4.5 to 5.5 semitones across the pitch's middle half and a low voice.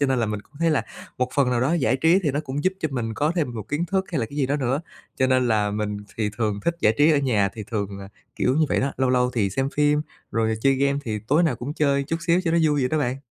Yes: average, 4.8 semitones; low, 130 Hz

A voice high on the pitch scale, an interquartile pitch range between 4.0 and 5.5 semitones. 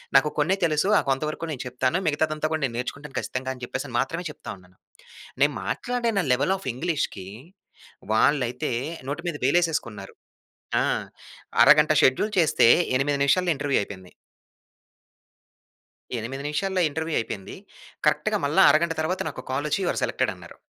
No: medium, 145 Hz; average, 4.3 semitones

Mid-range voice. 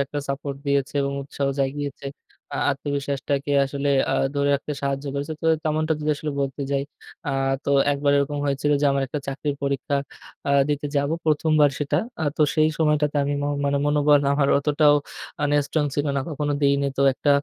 Yes: medium, 145 Hz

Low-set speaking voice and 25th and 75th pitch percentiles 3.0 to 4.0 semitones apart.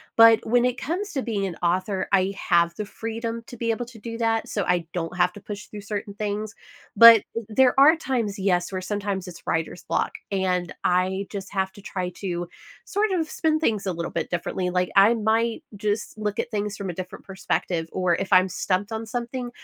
No: high, 205 Hz; average, 3.7 semitones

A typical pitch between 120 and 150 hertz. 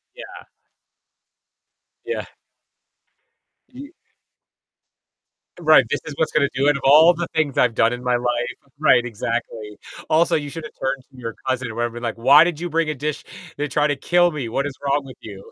Yes: medium, 140 Hz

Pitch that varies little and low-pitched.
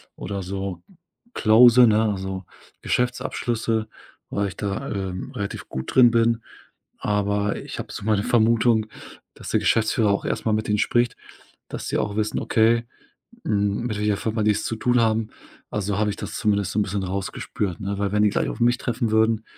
Yes: narrow, 2.1 semitones; low, 105 Hz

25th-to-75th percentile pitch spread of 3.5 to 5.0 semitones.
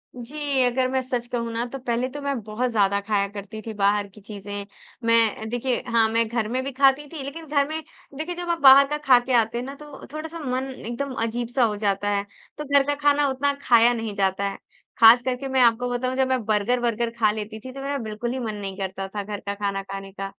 Yes: average, 4.1 semitones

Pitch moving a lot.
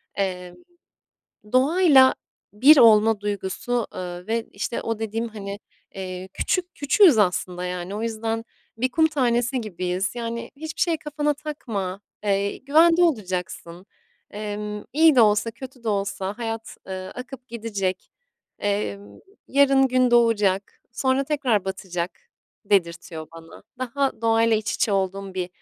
No: average, 4.9 semitones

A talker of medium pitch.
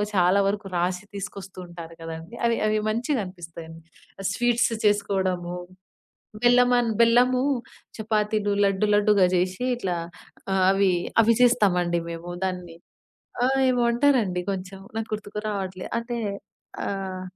No: high, 200 Hz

